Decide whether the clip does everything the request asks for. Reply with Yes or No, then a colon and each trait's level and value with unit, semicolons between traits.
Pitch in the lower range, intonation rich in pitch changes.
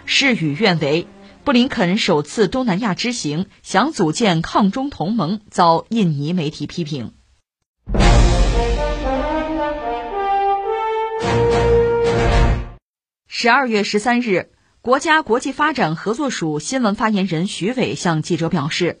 No: high, 200 Hz; wide, 7.6 semitones